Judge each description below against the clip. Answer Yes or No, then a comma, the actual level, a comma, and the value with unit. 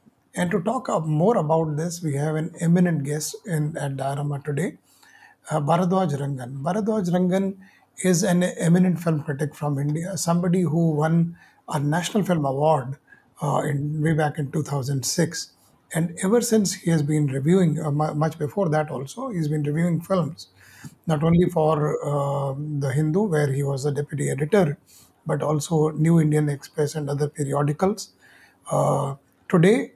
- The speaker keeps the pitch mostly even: No, average, 3.3 semitones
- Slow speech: No, average, 155 wpm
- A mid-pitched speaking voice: Yes, medium, 155 Hz